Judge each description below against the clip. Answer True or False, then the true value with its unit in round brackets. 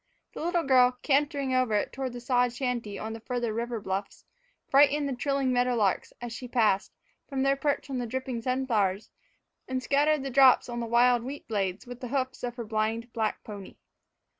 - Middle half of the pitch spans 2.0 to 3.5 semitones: True (2.7 semitones)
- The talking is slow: False (195 wpm)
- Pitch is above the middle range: True (245 Hz)